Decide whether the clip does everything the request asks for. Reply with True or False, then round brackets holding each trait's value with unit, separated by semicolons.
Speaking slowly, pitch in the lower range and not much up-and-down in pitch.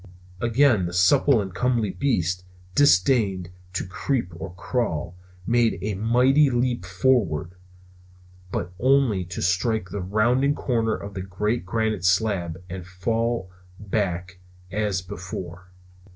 False (125 wpm; 100 Hz; 4.6 semitones)